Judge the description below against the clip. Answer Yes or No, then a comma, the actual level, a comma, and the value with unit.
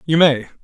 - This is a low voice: No, medium, 150 Hz